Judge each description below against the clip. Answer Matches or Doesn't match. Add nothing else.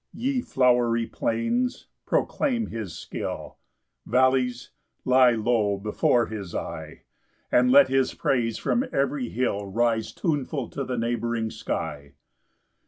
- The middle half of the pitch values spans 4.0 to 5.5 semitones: Doesn't match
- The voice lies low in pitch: Matches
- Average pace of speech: Doesn't match